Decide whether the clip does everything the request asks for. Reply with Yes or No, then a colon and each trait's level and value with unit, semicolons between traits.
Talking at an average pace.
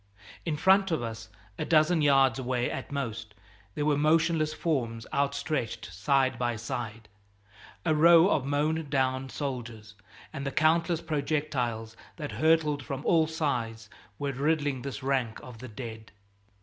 Yes: average, 145 wpm